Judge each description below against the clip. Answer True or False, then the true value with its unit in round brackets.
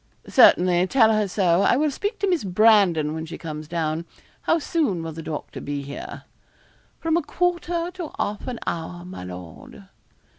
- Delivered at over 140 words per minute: True (175 wpm)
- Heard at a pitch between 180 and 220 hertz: True (185 Hz)